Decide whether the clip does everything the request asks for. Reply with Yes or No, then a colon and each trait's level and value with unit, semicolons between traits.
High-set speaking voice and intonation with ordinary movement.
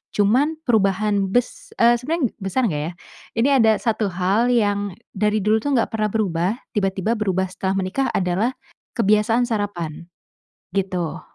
Yes: high, 210 Hz; average, 3.5 semitones